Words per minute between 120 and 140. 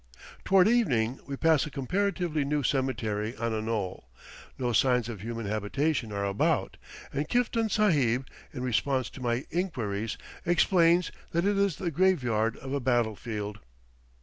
No: average, 150 wpm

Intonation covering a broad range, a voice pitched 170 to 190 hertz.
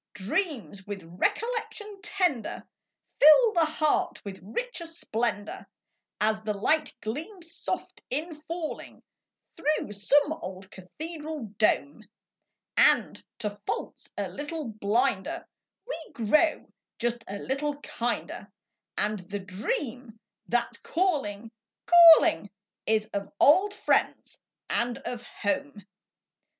No: wide, 7.8 semitones; very high, 260 Hz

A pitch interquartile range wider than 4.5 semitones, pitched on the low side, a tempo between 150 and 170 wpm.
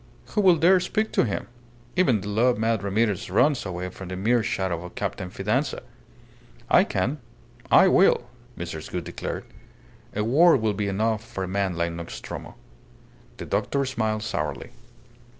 Yes: wide, 5.6 semitones; low, 110 Hz; average, 160 wpm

